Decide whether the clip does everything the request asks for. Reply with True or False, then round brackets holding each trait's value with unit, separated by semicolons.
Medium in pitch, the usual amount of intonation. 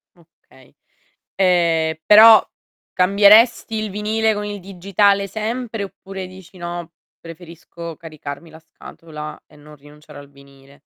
True (180 Hz; 4.4 semitones)